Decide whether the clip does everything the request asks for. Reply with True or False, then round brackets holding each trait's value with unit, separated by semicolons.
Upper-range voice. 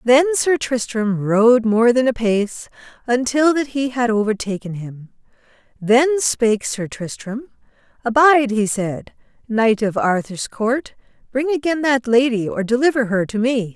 True (235 Hz)